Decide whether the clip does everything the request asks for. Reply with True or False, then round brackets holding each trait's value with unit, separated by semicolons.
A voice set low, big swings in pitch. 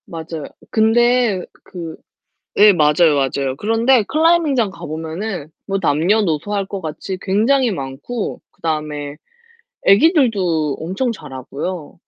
False (185 Hz; 6.4 semitones)